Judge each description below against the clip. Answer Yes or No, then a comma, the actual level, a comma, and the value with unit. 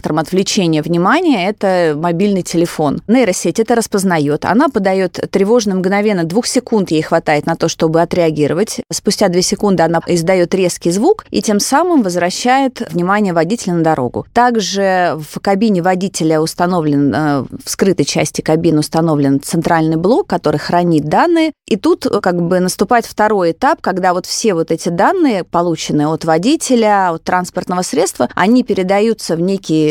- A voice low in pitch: No, medium, 180 Hz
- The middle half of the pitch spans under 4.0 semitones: No, average, 4.3 semitones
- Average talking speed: Yes, average, 145 wpm